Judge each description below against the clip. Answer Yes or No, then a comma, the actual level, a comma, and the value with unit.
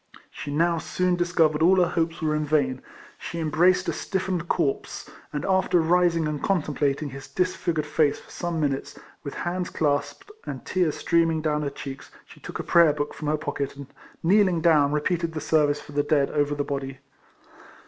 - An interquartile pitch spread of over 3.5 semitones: No, average, 3.0 semitones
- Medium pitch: Yes, medium, 155 Hz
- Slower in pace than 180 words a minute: No, average, 190 wpm